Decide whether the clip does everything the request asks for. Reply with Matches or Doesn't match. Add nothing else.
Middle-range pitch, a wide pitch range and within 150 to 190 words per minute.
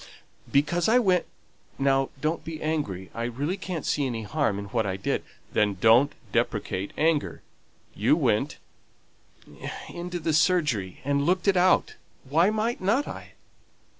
Matches